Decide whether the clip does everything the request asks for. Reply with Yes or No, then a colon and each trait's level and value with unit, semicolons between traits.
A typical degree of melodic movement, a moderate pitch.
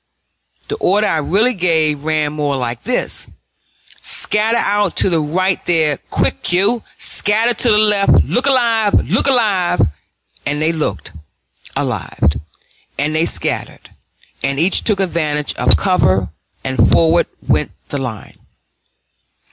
No: wide, 5.9 semitones; medium, 175 Hz